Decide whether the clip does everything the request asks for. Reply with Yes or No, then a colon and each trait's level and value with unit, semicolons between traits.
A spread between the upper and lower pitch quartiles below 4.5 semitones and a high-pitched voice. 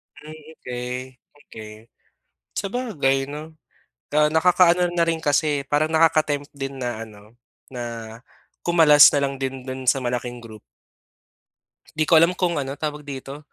No: average, 3.5 semitones; medium, 145 Hz